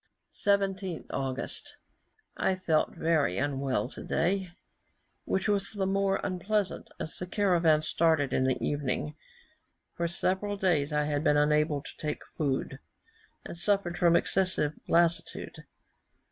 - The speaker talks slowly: Yes, slow, 130 wpm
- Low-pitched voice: No, medium, 170 Hz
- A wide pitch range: No, average, 4.5 semitones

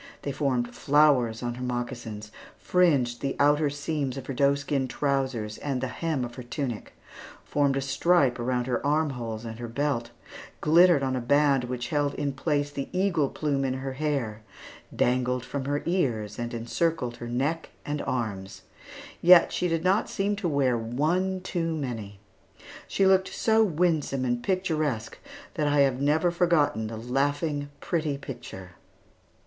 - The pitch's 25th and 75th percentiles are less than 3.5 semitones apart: No, average, 4.1 semitones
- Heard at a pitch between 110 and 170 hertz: Yes, medium, 140 Hz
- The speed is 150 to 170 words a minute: Yes, average, 160 wpm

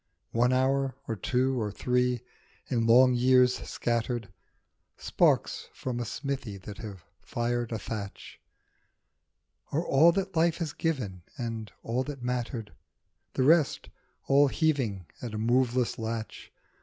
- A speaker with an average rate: No, slow, 130 wpm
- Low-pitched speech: Yes, low, 125 Hz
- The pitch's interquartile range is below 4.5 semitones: Yes, average, 2.8 semitones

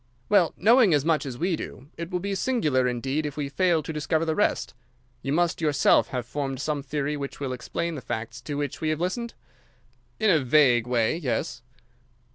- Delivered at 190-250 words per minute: Yes, average, 200 wpm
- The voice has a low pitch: No, medium, 150 Hz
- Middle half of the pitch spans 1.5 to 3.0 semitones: No, average, 4.1 semitones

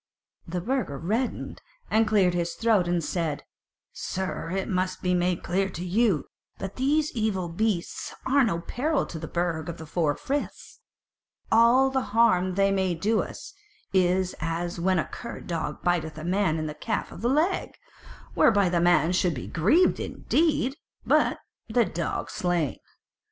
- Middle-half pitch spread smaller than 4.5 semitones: No, average, 4.8 semitones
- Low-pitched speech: No, medium, 185 Hz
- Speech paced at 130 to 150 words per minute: No, average, 165 wpm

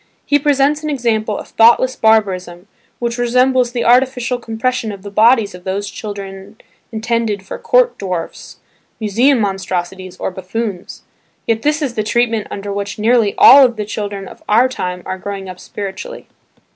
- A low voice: No, high, 220 Hz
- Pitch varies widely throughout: No, average, 3.8 semitones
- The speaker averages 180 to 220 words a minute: No, average, 160 wpm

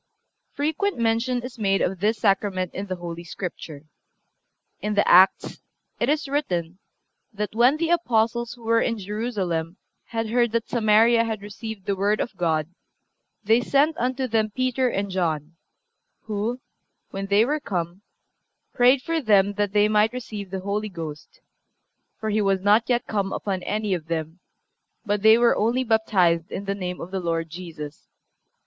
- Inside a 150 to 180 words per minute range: Yes, average, 165 wpm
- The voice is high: Yes, high, 210 Hz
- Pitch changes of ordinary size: Yes, average, 4.1 semitones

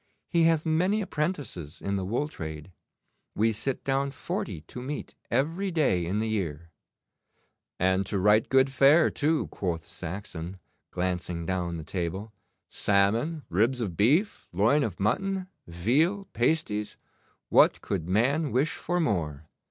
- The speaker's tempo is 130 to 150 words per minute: Yes, average, 140 wpm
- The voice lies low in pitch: Yes, low, 110 Hz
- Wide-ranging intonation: Yes, wide, 8.6 semitones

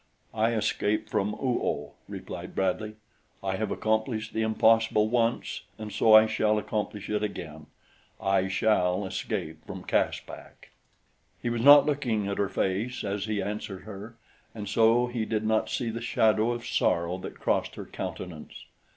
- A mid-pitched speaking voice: No, low, 110 Hz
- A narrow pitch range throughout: Yes, narrow, 2.3 semitones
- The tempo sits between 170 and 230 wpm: No, average, 160 wpm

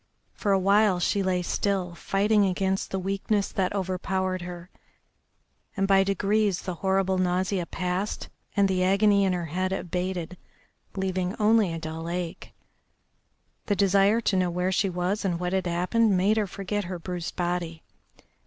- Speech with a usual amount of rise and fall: No, narrow, 1.8 semitones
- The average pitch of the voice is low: No, high, 190 Hz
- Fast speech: No, average, 160 wpm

